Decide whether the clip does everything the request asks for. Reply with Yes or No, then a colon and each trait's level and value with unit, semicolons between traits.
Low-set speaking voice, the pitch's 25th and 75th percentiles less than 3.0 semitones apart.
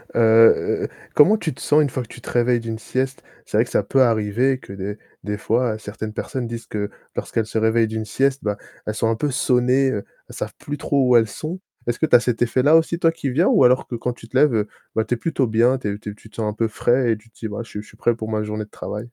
No: low, 115 Hz; average, 3.3 semitones